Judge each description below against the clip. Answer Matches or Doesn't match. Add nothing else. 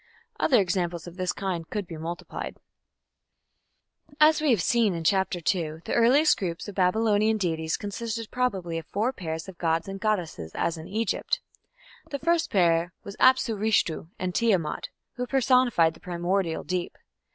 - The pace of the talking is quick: Doesn't match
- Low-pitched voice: Doesn't match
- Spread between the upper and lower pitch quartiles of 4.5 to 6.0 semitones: Matches